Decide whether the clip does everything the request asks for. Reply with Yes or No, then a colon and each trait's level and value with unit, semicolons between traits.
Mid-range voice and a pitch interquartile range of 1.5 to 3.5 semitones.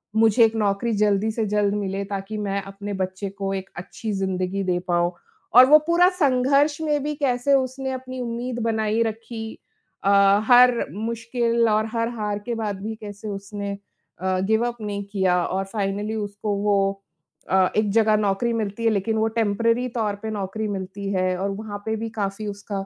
No: high, 215 Hz; average, 2.8 semitones